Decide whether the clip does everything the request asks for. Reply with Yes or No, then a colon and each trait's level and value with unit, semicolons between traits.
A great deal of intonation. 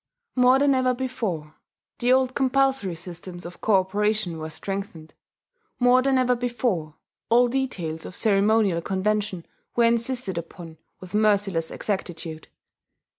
Yes: wide, 6.1 semitones